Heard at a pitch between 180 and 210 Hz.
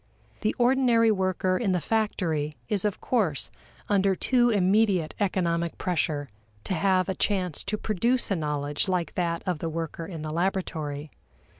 Yes: medium, 185 Hz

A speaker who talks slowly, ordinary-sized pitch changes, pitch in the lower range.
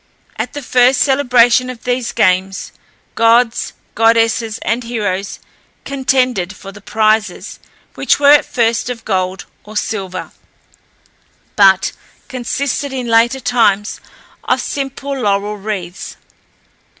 No: slow, 115 wpm; average, 3.8 semitones; high, 230 Hz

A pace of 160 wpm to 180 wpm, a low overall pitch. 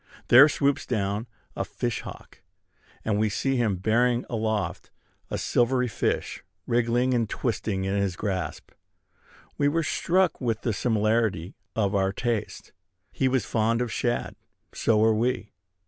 No: average, 145 wpm; low, 115 Hz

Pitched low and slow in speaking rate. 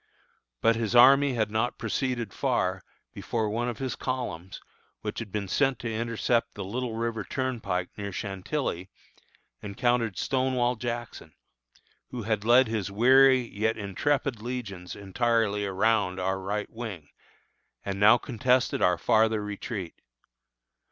Yes: low, 110 Hz; slow, 130 wpm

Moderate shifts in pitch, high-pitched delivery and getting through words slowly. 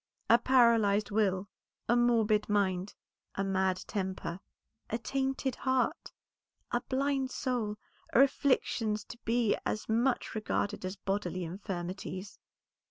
Yes: average, 3.9 semitones; high, 215 Hz; slow, 115 wpm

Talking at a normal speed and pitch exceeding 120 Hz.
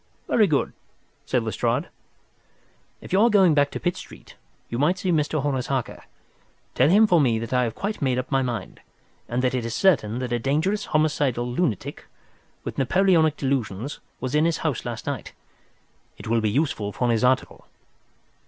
Yes: average, 180 wpm; low, 135 Hz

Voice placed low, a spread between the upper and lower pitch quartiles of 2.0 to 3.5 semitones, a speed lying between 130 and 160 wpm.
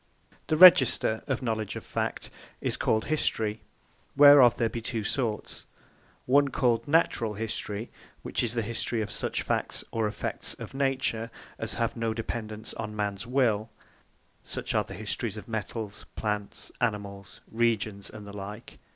Yes: low, 110 Hz; narrow, 2.4 semitones; average, 155 wpm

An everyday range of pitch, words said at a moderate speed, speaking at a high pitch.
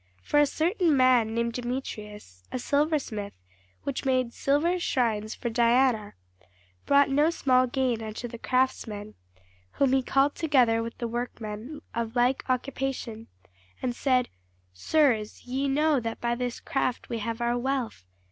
Yes: average, 3.0 semitones; average, 145 wpm; very high, 250 Hz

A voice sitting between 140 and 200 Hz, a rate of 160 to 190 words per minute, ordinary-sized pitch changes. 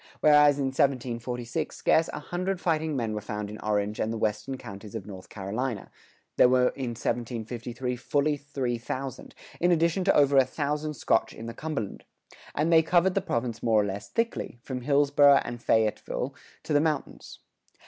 No: low, 130 Hz; average, 175 wpm; average, 4.6 semitones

